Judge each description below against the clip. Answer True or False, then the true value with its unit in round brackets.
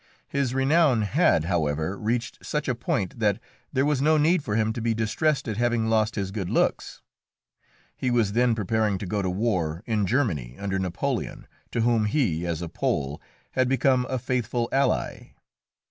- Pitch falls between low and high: False (110 Hz)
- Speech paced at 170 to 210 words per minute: True (175 wpm)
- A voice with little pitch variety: False (4.8 semitones)